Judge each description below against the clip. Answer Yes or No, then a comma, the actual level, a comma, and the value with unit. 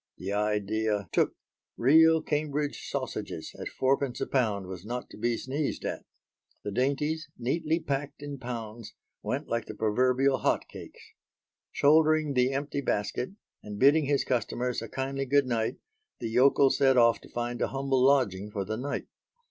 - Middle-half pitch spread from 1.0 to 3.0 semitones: No, average, 4.1 semitones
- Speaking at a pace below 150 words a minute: No, average, 155 wpm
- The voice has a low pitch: Yes, low, 130 Hz